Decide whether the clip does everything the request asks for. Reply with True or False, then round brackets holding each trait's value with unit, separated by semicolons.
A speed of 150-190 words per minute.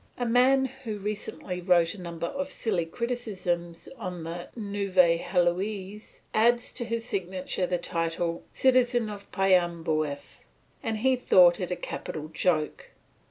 False (135 wpm)